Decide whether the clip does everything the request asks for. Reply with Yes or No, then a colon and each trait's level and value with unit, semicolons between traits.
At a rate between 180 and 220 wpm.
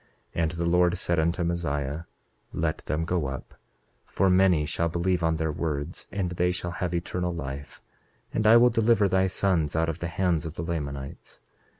Yes: average, 190 wpm